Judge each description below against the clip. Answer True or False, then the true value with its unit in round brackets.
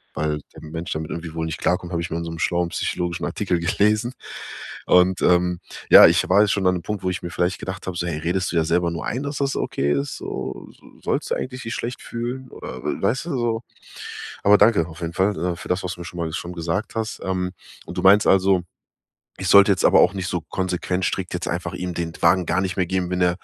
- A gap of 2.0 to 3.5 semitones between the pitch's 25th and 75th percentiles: True (2.6 semitones)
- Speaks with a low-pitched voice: True (90 Hz)